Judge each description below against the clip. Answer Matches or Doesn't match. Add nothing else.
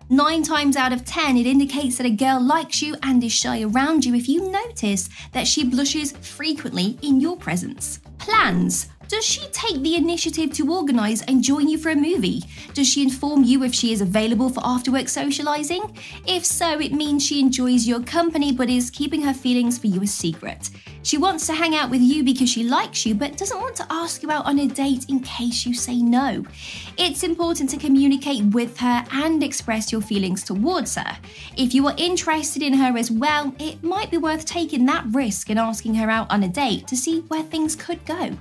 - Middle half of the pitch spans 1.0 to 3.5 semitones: Doesn't match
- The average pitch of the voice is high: Matches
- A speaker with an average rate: Doesn't match